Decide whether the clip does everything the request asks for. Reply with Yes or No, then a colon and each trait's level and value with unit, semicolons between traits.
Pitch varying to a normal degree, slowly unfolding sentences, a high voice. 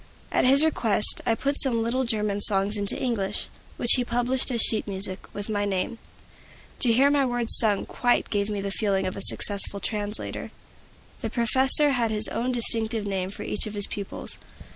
No: average, 3.2 semitones; average, 185 wpm; high, 220 Hz